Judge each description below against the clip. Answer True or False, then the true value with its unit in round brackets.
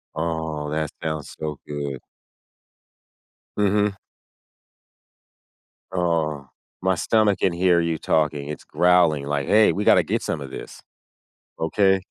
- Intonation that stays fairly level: False (3.8 semitones)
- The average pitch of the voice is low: True (80 Hz)